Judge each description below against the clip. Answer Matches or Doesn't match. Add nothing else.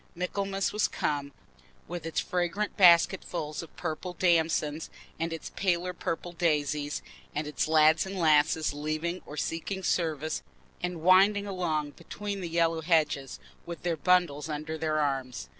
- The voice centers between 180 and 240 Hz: Doesn't match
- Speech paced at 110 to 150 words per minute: Matches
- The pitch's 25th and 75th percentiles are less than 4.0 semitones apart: Matches